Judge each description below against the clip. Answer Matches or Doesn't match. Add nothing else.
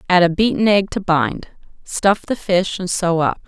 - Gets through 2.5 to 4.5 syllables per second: Matches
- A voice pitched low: Doesn't match